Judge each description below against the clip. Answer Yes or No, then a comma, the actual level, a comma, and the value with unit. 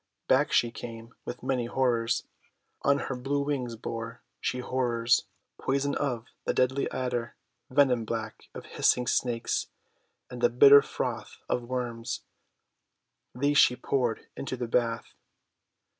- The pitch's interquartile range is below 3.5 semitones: Yes, narrow, 2.4 semitones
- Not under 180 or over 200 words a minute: No, slow, 135 wpm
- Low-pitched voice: Yes, low, 125 Hz